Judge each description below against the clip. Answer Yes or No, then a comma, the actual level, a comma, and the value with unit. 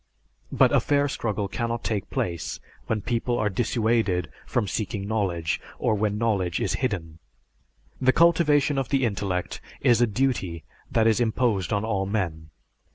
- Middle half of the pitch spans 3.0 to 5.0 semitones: Yes, average, 3.9 semitones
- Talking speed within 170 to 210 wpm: No, average, 155 wpm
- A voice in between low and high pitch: No, low, 110 Hz